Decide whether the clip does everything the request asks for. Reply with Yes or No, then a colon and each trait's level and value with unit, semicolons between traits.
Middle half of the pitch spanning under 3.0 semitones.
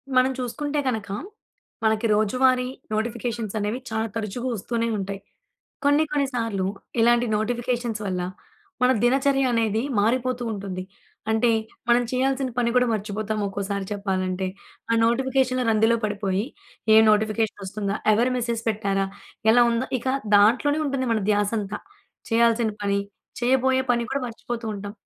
No: average, 3.3 semitones